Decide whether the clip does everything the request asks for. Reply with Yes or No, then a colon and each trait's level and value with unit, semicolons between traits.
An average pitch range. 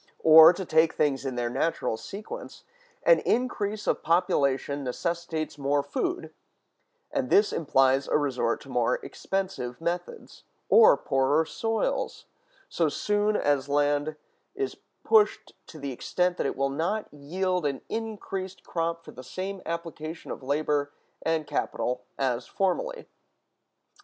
No: wide, 5.7 semitones